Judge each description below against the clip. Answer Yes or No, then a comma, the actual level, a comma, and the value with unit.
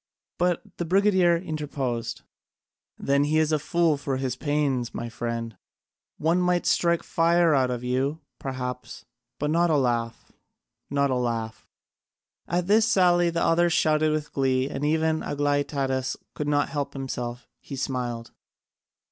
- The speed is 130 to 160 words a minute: Yes, average, 150 wpm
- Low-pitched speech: No, medium, 145 Hz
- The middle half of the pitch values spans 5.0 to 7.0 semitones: No, average, 4.3 semitones